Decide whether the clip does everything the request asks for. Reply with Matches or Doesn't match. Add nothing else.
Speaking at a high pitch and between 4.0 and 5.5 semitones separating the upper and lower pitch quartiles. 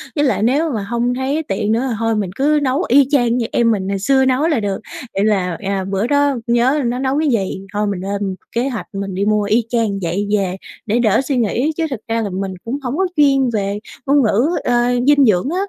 Matches